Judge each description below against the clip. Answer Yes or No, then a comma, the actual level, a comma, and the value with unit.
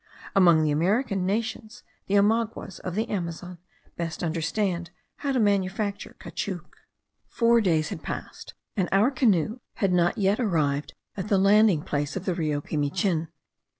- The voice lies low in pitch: No, high, 190 Hz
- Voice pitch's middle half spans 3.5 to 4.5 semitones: Yes, average, 4.2 semitones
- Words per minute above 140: Yes, average, 150 wpm